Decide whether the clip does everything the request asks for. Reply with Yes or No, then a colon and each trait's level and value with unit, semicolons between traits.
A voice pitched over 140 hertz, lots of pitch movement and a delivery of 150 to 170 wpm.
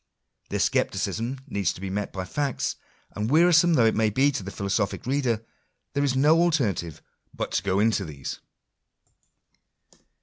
No: low, 115 Hz; wide, 6.3 semitones; average, 160 wpm